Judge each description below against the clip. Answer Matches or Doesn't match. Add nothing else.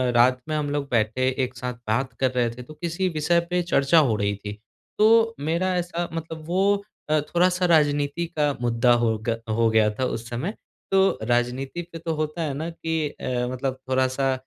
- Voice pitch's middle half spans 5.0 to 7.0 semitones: Matches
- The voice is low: Doesn't match